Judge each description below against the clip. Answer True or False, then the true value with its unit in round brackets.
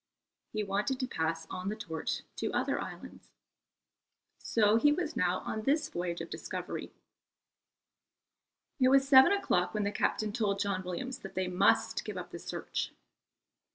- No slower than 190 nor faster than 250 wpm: False (155 wpm)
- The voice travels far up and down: True (6.2 semitones)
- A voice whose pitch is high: True (210 Hz)